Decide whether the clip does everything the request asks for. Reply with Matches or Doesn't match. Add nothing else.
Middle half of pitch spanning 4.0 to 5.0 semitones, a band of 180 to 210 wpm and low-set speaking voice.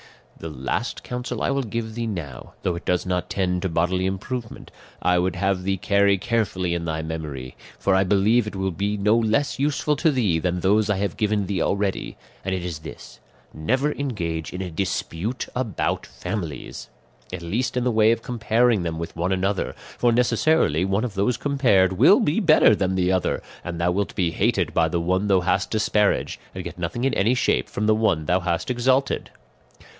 Matches